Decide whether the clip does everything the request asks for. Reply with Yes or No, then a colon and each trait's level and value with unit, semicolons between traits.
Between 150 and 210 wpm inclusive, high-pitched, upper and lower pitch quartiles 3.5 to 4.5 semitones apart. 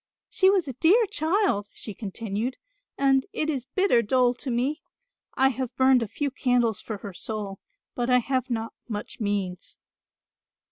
Yes: average, 160 wpm; very high, 250 Hz; average, 3.8 semitones